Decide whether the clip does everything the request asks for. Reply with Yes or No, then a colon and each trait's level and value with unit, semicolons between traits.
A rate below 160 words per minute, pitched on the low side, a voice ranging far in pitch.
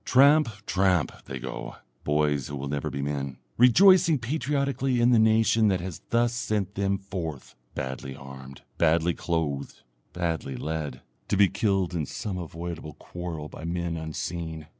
Yes: average, 150 wpm; very low, 85 Hz; wide, 6.6 semitones